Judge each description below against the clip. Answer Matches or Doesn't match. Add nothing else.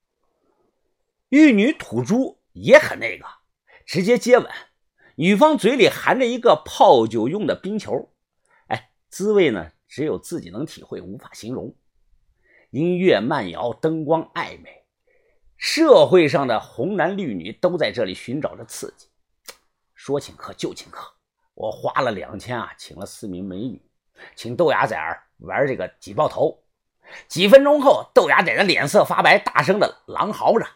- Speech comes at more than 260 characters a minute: Doesn't match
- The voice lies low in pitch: Doesn't match